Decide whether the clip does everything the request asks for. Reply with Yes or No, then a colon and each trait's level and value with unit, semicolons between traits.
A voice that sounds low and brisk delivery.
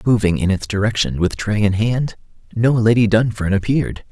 No: low, 110 Hz; average, 175 wpm